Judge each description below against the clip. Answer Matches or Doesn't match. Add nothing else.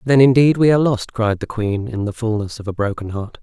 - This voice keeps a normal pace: Doesn't match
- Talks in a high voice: Doesn't match